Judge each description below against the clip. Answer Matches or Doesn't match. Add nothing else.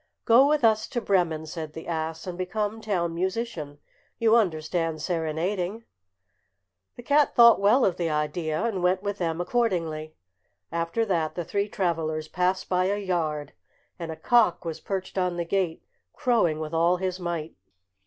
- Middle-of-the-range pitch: Matches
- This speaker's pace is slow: Doesn't match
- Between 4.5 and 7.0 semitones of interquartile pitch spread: Doesn't match